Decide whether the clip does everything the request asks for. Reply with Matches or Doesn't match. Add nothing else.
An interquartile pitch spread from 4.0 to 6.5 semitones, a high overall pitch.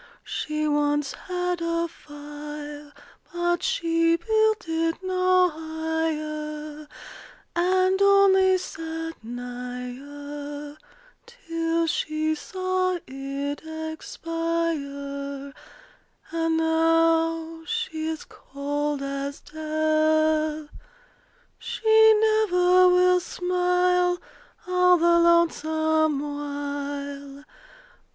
Doesn't match